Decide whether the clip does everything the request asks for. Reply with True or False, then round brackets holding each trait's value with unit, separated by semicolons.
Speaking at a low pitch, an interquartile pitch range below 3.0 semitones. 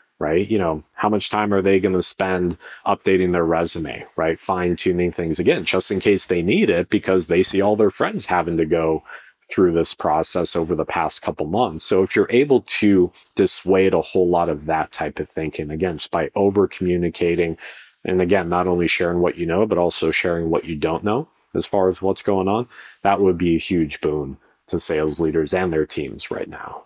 True (90 Hz; 2.4 semitones)